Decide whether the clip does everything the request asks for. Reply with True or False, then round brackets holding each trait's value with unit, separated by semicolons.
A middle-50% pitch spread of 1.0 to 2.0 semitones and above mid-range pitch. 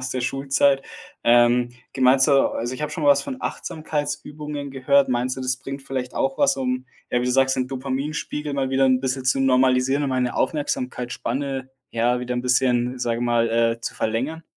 False (1.7 semitones; 130 Hz)